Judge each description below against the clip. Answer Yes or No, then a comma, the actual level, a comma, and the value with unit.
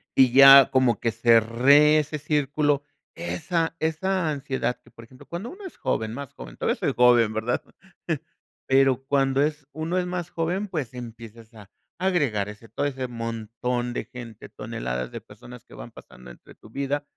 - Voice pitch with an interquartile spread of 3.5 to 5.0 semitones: Yes, average, 4.7 semitones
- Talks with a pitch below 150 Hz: Yes, low, 135 Hz